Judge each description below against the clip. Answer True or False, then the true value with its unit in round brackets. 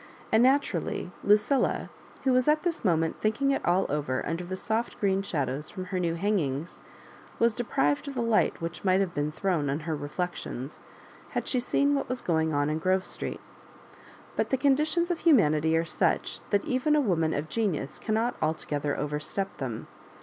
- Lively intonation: True (7.5 semitones)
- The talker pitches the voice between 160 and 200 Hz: True (185 Hz)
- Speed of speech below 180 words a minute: False (185 wpm)